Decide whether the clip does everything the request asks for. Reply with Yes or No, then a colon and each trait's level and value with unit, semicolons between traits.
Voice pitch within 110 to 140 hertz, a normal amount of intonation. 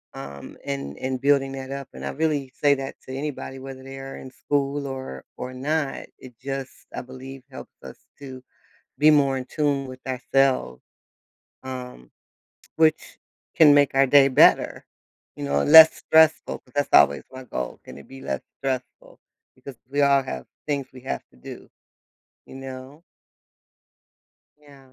No: low, 135 Hz; narrow, 1.7 semitones